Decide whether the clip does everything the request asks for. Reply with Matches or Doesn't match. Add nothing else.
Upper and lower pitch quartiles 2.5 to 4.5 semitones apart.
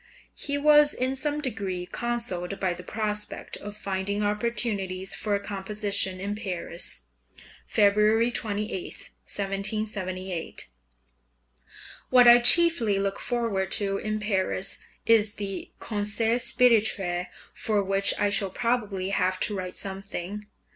Matches